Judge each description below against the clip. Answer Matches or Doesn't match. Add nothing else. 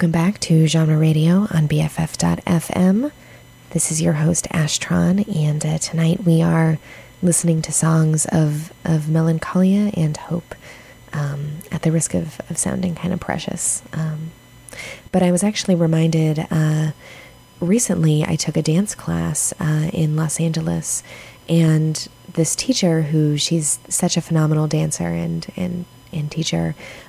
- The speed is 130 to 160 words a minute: Matches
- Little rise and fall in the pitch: Matches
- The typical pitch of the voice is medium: Matches